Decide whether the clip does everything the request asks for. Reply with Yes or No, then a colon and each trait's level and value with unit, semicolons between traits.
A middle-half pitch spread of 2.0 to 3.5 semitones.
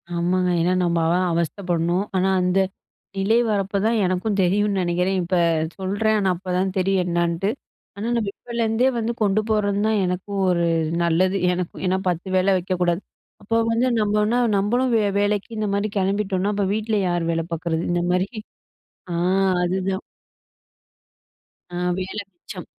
Yes: narrow, 2.6 semitones